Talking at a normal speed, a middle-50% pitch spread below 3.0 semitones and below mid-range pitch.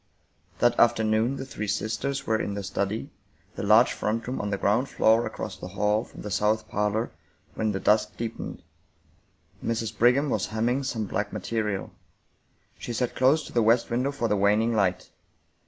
Yes: average, 175 wpm; narrow, 2.4 semitones; low, 110 Hz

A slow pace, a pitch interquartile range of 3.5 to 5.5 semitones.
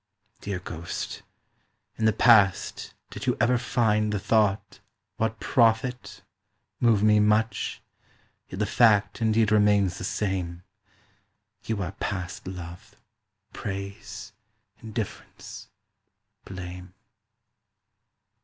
No: slow, 100 wpm; average, 2.7 semitones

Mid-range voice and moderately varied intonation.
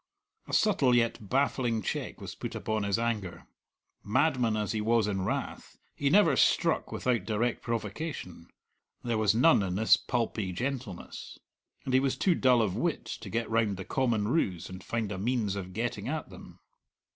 No: low, 115 Hz; average, 3.7 semitones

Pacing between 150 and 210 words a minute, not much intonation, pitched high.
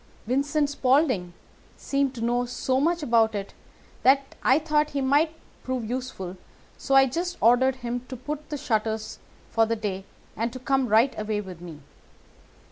No: average, 170 wpm; average, 4.0 semitones; very high, 255 Hz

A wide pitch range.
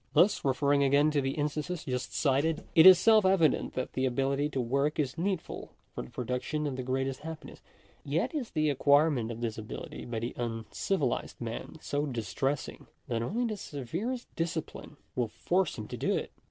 No: average, 4.3 semitones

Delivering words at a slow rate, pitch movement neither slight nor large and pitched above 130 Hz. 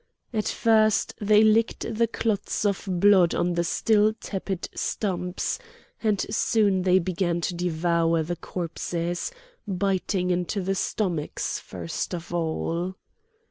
Yes: slow, 125 wpm; average, 3.2 semitones; medium, 185 Hz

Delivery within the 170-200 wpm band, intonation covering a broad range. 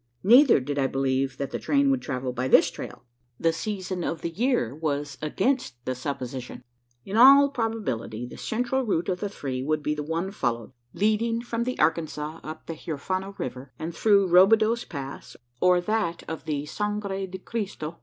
Yes: average, 180 wpm; wide, 7.2 semitones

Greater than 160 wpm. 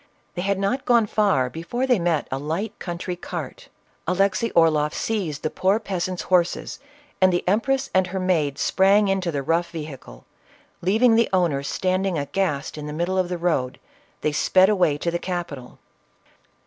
Yes: average, 170 wpm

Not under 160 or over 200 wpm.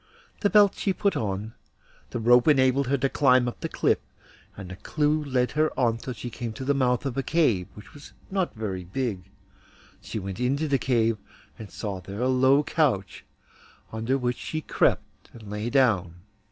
Yes: average, 190 wpm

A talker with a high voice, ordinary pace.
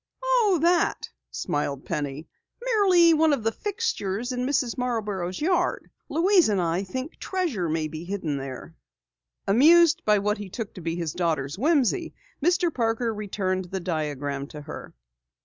Yes: high, 215 Hz; average, 150 wpm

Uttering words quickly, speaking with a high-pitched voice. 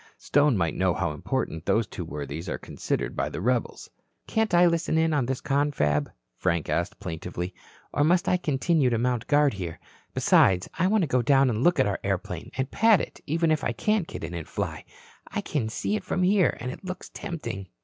No: fast, 210 wpm; low, 130 Hz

